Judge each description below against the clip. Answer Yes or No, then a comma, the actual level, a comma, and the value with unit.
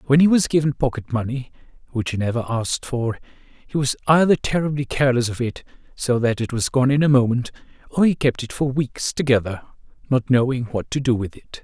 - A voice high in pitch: No, low, 130 Hz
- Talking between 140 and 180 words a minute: No, fast, 205 wpm